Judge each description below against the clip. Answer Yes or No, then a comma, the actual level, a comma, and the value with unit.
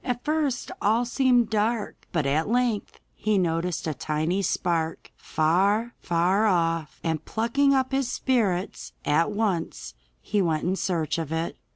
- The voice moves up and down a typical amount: No, wide, 6.1 semitones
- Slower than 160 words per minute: Yes, average, 150 wpm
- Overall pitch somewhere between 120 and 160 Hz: No, high, 195 Hz